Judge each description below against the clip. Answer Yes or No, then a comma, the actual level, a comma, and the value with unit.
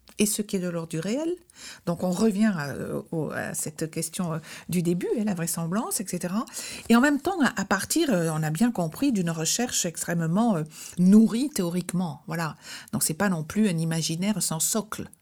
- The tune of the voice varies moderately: Yes, average, 4.7 semitones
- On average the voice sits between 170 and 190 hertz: Yes, medium, 185 Hz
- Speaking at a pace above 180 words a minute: No, average, 175 wpm